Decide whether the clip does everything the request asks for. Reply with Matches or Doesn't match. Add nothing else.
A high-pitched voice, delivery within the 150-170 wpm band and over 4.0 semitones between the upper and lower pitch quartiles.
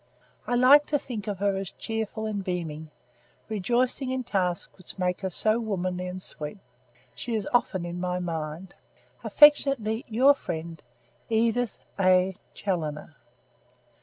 Doesn't match